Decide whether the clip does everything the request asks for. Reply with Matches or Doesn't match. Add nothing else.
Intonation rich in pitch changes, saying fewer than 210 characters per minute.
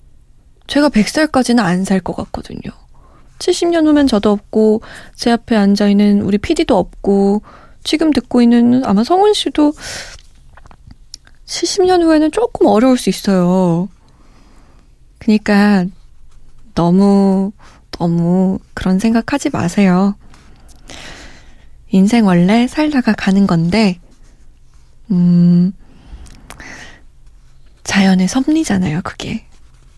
Matches